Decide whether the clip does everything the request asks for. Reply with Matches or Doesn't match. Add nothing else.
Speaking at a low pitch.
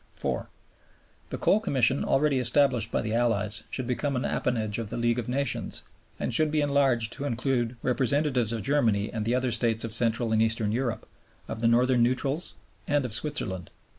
Matches